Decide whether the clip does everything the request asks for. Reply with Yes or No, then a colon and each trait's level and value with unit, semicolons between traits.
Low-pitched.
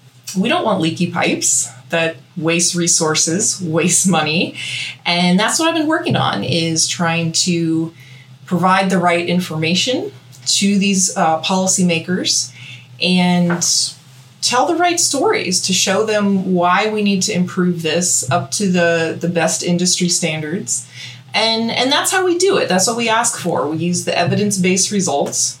No: medium, 175 Hz